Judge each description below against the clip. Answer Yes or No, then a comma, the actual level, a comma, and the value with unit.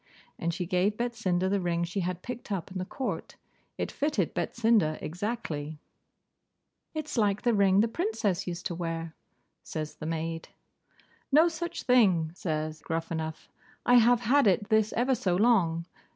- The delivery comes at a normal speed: Yes, average, 155 wpm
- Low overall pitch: No, high, 190 Hz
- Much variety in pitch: Yes, wide, 6.0 semitones